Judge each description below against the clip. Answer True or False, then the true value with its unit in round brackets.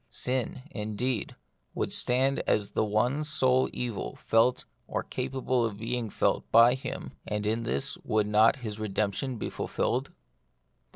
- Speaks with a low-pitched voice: True (115 Hz)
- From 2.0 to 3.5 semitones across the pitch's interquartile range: True (3.1 semitones)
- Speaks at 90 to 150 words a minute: True (140 wpm)